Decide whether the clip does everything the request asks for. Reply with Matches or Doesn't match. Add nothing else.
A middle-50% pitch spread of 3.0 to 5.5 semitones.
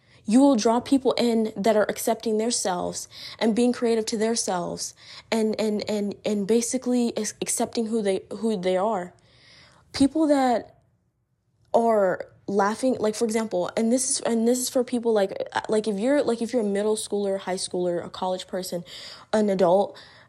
Matches